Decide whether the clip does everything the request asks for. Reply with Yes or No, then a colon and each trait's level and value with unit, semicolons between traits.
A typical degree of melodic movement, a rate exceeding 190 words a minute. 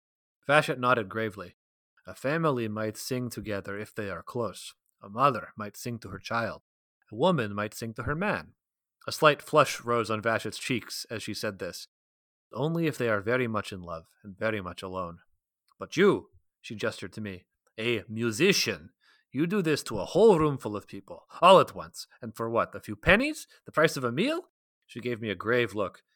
Yes: average, 3.9 semitones; average, 200 wpm